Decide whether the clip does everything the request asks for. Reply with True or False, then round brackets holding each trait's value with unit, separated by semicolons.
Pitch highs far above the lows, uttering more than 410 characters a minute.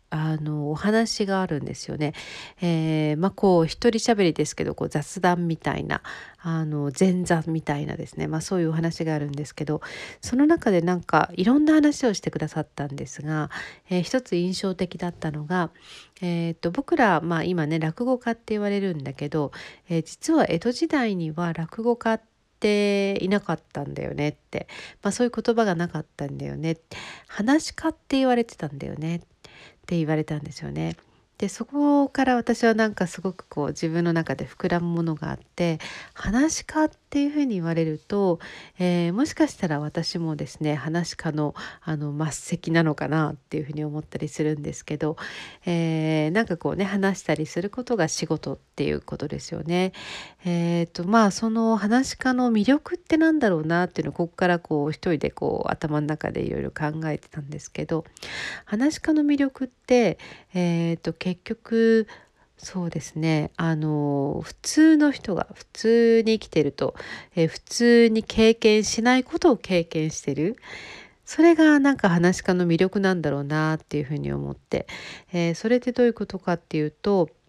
False (6.1 semitones; 360 characters per minute)